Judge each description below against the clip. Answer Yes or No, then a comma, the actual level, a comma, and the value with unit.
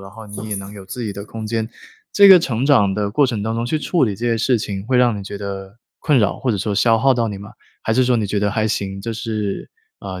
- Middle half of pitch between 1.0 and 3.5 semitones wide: Yes, average, 3.1 semitones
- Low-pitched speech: Yes, low, 110 Hz